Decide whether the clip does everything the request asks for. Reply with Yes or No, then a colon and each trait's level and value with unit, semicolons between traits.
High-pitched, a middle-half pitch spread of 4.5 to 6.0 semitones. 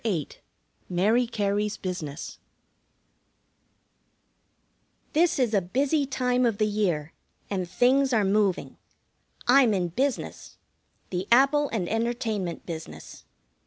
Yes: high, 215 Hz; average, 5.3 semitones